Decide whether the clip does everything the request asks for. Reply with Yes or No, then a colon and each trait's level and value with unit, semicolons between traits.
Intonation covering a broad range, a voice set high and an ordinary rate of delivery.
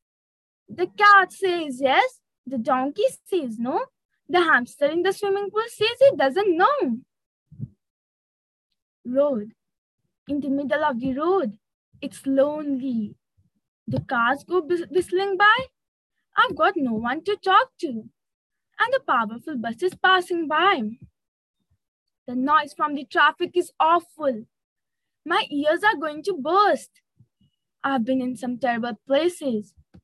Yes: wide, 6.3 semitones; very high, 305 Hz; average, 130 wpm